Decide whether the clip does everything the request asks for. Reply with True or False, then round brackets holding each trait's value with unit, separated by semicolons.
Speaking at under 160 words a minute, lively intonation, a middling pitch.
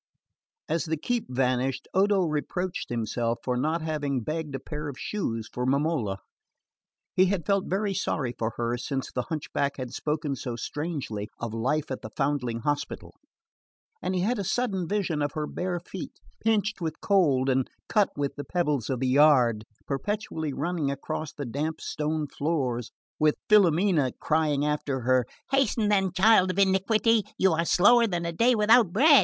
False (170 wpm; 6.1 semitones; 155 Hz)